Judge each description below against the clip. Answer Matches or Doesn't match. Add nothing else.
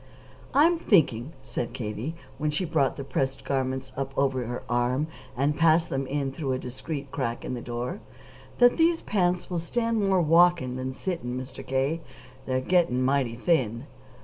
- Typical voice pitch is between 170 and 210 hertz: Doesn't match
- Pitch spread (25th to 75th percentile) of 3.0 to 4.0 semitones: Doesn't match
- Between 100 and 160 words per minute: Doesn't match